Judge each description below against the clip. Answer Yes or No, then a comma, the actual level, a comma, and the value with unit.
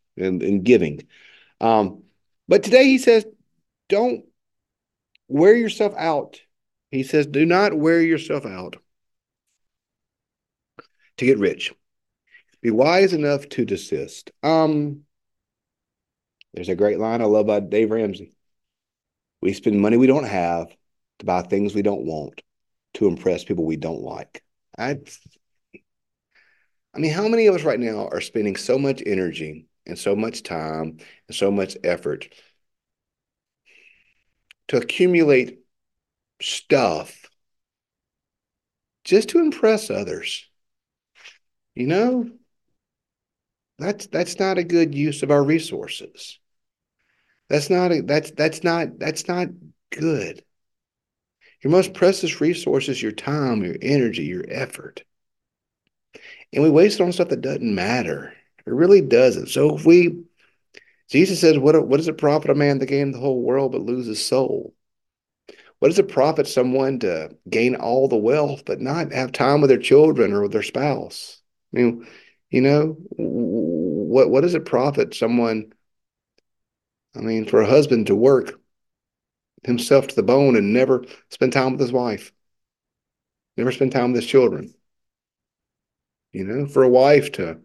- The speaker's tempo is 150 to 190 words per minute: No, average, 140 wpm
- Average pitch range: No, wide, 7.7 semitones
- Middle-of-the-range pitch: Yes, medium, 145 Hz